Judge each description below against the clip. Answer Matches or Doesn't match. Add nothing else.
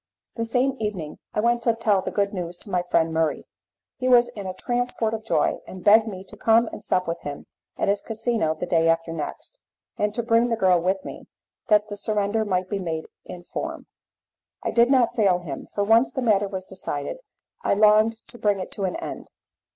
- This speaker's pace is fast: Matches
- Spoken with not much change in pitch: Doesn't match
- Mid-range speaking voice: Doesn't match